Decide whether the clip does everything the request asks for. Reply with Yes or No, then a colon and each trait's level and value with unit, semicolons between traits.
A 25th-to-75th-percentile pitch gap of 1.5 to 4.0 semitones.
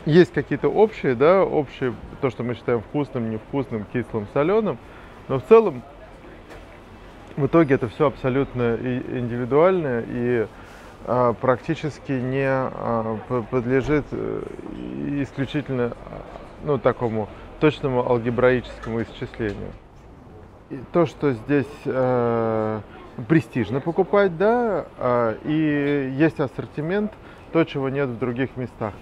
Yes: average, 3.7 semitones